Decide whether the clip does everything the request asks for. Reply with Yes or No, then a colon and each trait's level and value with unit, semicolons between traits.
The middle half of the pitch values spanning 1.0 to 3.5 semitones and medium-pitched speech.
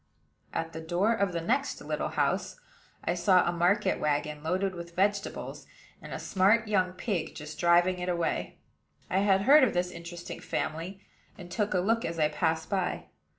Yes: average, 2.8 semitones; medium, 180 Hz